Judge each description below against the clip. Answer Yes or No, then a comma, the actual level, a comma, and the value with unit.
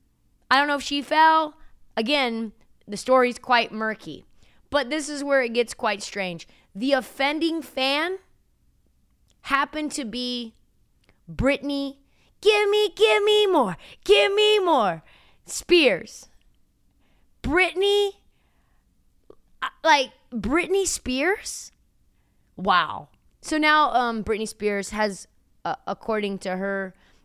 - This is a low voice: No, very high, 275 Hz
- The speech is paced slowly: Yes, slow, 110 wpm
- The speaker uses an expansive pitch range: Yes, wide, 6.2 semitones